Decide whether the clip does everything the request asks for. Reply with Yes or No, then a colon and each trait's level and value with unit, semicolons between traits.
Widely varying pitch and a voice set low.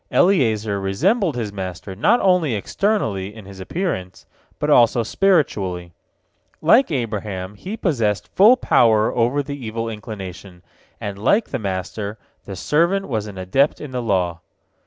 Yes: wide, 7.7 semitones; low, 110 Hz